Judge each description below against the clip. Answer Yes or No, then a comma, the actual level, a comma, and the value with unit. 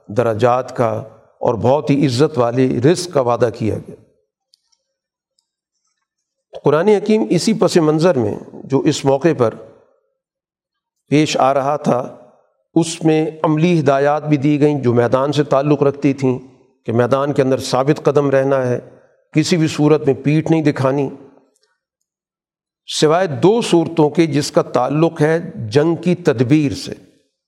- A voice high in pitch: No, medium, 150 Hz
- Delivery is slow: No, average, 145 wpm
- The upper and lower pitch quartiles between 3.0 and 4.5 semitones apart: Yes, average, 4.0 semitones